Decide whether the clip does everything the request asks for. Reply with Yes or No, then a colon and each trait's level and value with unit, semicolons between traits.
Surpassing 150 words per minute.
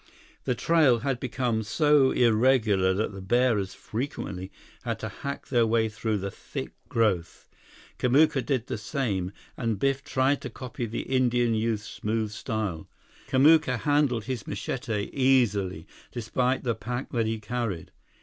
No: average, 145 wpm